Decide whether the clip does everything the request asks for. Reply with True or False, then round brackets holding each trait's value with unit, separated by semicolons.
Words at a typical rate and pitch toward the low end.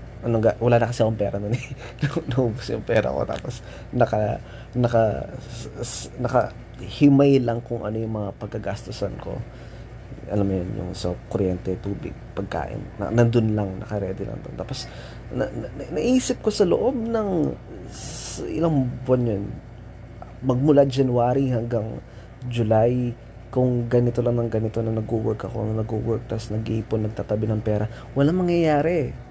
True (145 wpm; 115 Hz)